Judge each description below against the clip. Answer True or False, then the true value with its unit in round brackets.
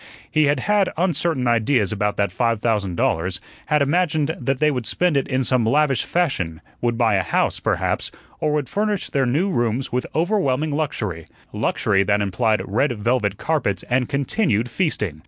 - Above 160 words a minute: True (175 wpm)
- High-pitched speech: False (125 Hz)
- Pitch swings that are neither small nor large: False (6.1 semitones)